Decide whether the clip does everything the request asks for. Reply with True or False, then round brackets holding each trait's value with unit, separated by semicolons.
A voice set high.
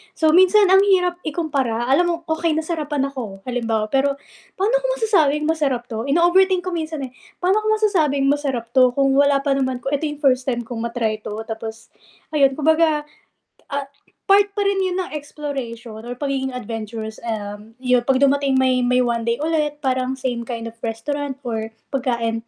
True (275 Hz)